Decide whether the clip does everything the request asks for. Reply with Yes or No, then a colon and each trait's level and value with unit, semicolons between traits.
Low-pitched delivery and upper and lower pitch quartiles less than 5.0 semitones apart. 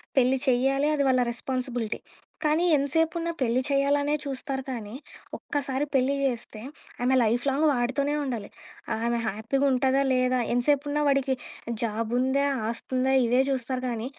No: very high, 260 Hz; narrow, 2.4 semitones